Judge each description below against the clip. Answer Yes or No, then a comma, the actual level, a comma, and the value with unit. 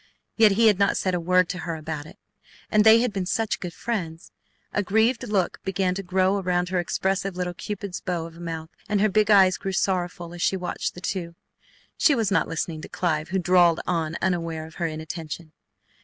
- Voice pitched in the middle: Yes, medium, 180 Hz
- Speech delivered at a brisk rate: Yes, fast, 215 wpm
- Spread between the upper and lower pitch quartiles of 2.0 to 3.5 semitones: Yes, average, 2.7 semitones